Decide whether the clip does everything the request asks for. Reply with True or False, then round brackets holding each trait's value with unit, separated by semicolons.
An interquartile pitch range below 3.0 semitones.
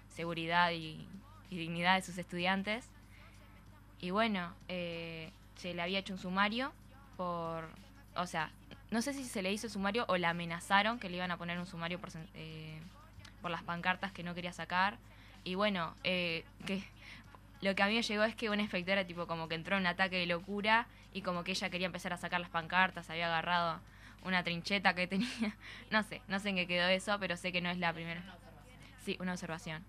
True (2.6 semitones)